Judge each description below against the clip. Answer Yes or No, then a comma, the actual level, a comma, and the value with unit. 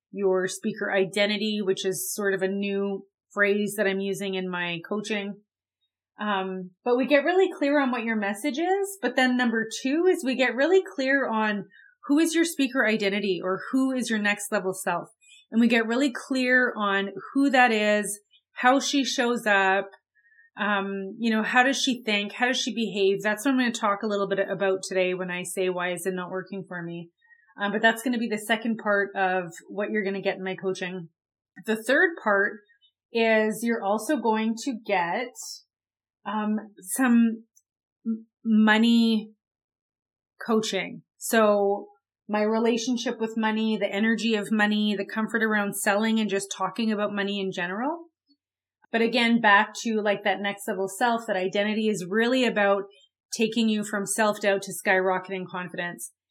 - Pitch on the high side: Yes, high, 210 Hz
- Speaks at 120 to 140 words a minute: No, average, 175 wpm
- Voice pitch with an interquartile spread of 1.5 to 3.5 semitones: Yes, average, 3.1 semitones